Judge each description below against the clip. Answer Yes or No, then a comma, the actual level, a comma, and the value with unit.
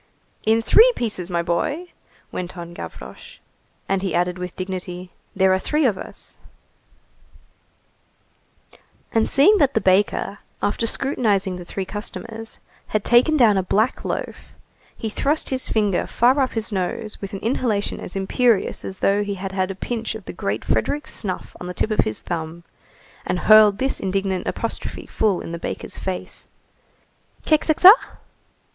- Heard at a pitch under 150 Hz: No, high, 205 Hz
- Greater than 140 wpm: Yes, average, 160 wpm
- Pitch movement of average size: Yes, average, 4.2 semitones